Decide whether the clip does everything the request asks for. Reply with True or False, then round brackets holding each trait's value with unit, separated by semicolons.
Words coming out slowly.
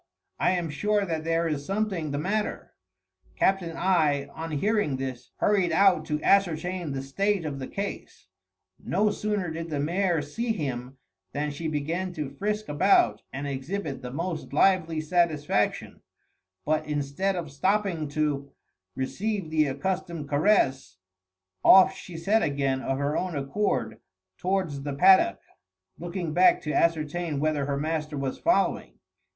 False (145 wpm)